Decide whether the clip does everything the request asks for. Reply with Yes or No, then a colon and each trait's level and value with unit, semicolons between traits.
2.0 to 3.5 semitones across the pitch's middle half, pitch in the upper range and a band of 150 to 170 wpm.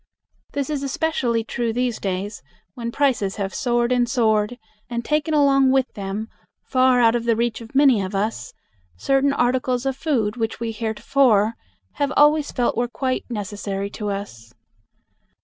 No: average, 4.0 semitones; high, 235 Hz; average, 160 wpm